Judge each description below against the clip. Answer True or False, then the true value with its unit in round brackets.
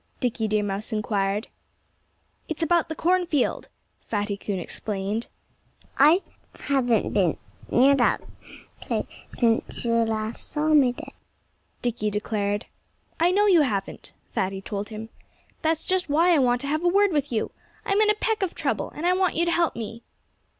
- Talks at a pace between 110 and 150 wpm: False (165 wpm)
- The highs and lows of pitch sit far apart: True (7.8 semitones)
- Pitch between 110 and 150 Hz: False (245 Hz)